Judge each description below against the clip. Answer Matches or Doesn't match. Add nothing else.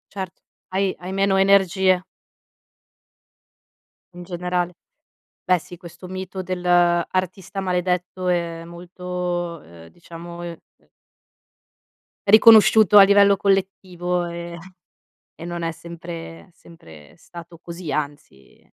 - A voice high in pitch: Doesn't match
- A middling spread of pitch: Doesn't match